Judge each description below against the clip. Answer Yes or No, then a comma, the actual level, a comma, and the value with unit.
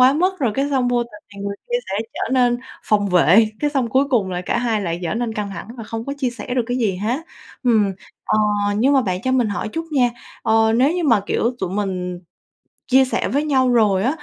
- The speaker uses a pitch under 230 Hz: No, high, 235 Hz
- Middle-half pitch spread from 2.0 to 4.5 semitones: Yes, average, 4.2 semitones